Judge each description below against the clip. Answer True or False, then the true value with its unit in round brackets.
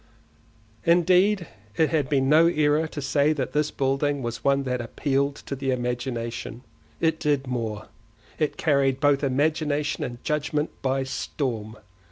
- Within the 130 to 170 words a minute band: True (140 wpm)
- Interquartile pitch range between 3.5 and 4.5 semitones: False (3.1 semitones)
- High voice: False (140 Hz)